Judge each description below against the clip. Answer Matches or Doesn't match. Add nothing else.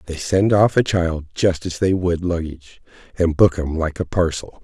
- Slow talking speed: Doesn't match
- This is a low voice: Matches